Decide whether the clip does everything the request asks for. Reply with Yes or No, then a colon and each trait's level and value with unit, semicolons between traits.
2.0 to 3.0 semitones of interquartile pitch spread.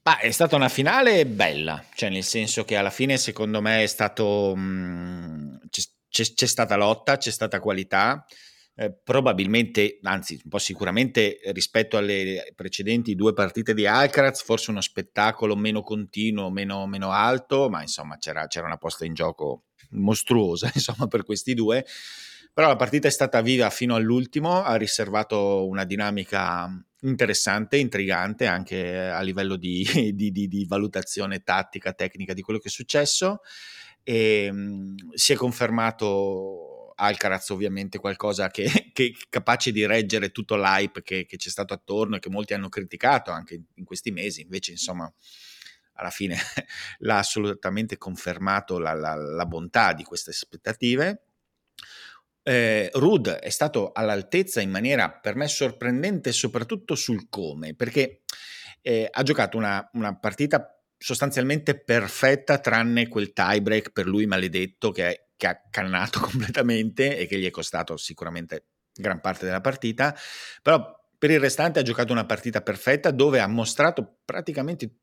No: average, 4.2 semitones